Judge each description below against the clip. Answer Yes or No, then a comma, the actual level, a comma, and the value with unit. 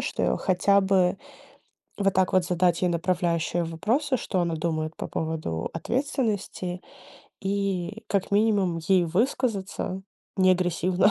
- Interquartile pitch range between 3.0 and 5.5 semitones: No, narrow, 2.5 semitones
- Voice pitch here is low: No, medium, 185 Hz